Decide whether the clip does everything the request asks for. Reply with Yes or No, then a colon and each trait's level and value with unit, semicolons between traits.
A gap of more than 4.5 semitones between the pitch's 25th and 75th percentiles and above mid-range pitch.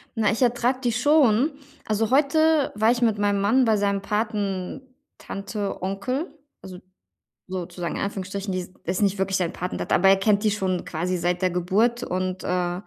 No: average, 4.2 semitones; high, 200 Hz